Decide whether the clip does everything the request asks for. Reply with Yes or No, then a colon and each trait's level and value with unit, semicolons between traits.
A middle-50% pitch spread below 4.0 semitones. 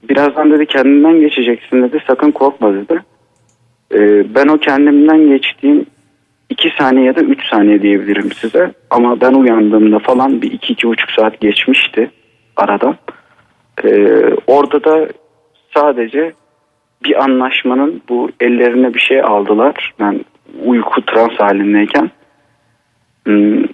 No: average, 4.7 semitones